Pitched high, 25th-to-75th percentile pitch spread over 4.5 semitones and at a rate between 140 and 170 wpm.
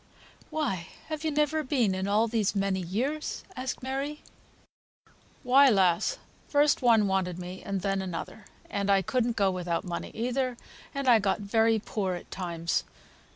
Yes: high, 210 Hz; wide, 5.5 semitones; average, 155 wpm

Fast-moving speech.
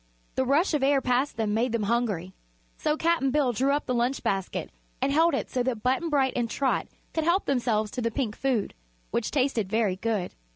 Yes: fast, 210 wpm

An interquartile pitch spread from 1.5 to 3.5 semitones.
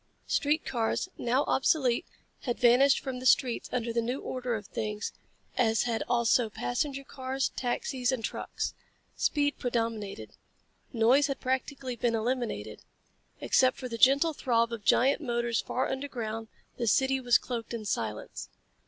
Yes: narrow, 2.5 semitones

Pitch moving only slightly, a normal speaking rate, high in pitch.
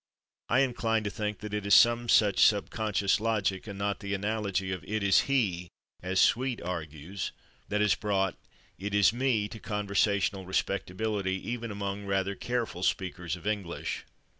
No: narrow, 2.3 semitones; average, 160 wpm; low, 100 Hz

